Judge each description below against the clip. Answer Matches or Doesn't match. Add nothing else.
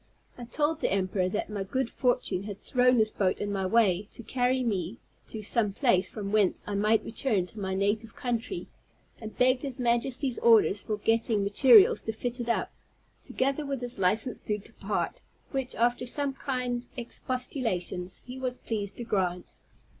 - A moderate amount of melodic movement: Matches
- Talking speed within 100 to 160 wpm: Doesn't match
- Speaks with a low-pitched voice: Doesn't match